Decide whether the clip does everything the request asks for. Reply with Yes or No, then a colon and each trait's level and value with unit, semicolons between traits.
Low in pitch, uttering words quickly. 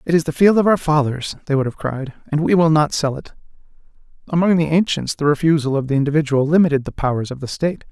No: medium, 150 Hz; fast, 235 wpm